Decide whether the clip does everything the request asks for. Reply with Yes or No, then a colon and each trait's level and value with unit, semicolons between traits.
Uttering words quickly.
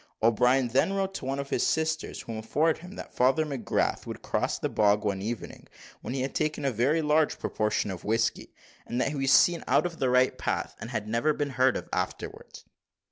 Yes: fast, 215 wpm